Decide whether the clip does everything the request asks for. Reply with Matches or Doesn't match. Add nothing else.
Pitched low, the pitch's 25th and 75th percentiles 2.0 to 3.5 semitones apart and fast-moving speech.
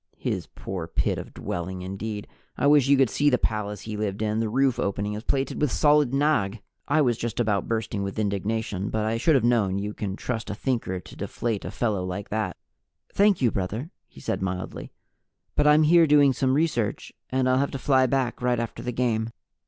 Doesn't match